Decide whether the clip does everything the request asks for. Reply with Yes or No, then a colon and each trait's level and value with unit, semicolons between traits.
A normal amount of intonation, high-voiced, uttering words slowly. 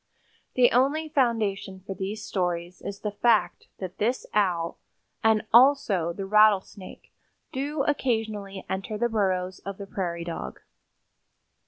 Yes: average, 3.9 semitones; high, 205 Hz; slow, 130 wpm